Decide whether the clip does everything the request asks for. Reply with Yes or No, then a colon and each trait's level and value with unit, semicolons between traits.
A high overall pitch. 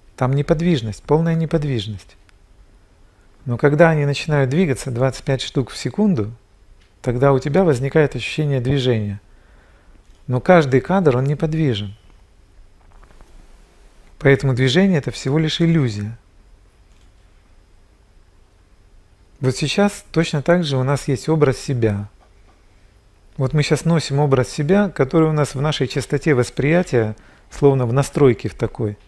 No: low, 130 Hz